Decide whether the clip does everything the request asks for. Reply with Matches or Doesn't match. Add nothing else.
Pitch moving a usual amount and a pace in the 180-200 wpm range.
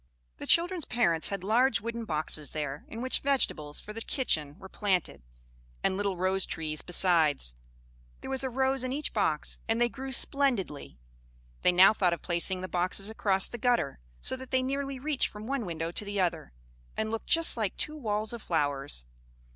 Doesn't match